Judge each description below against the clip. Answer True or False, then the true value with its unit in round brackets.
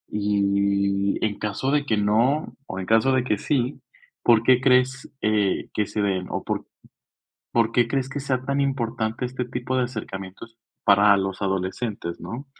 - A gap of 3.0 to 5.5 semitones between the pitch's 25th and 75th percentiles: True (4.2 semitones)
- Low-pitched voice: True (115 Hz)